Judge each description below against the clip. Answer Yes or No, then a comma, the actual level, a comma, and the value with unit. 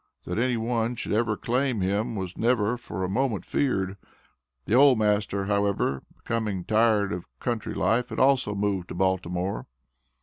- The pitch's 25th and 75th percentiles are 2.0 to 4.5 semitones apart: Yes, average, 3.7 semitones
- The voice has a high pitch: No, low, 105 Hz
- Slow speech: No, average, 160 wpm